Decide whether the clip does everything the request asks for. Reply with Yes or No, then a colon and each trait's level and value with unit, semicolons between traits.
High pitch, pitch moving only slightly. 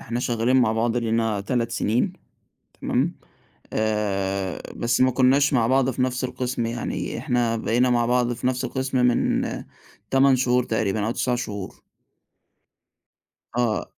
No: low, 120 Hz; narrow, 2.1 semitones